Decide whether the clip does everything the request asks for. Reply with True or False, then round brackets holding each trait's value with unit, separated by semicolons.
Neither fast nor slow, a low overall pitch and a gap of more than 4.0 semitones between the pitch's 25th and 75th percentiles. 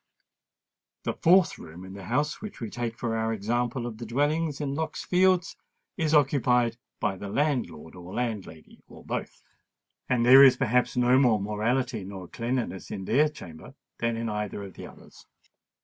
True (170 wpm; 120 Hz; 4.9 semitones)